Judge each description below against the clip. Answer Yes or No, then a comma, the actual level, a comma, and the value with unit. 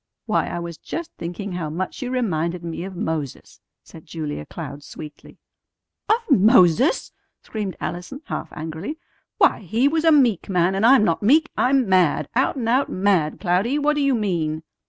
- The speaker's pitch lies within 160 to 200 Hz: Yes, high, 190 Hz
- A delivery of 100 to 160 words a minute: No, average, 175 wpm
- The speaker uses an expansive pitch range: Yes, wide, 7.4 semitones